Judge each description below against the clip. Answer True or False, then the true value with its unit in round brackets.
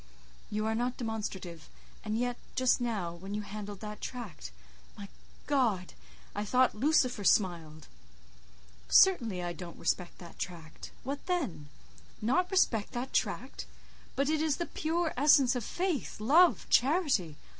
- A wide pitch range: True (7.1 semitones)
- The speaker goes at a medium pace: False (130 wpm)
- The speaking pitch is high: True (220 Hz)